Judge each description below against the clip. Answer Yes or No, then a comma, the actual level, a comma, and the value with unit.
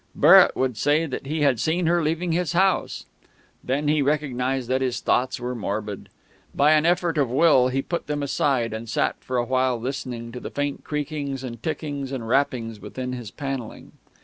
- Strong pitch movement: No, average, 3.3 semitones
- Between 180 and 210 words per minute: Yes, average, 190 wpm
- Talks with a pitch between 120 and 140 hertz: Yes, low, 135 Hz